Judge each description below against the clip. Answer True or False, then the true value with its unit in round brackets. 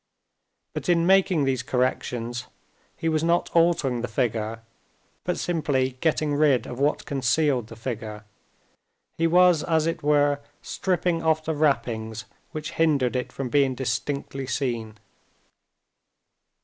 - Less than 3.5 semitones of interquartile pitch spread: False (4.7 semitones)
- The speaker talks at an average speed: False (130 wpm)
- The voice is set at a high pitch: False (140 Hz)